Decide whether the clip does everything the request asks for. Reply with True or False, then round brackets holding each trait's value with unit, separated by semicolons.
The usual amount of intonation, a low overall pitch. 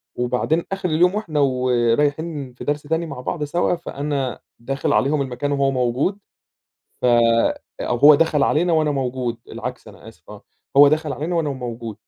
False (3.8 semitones; 145 Hz)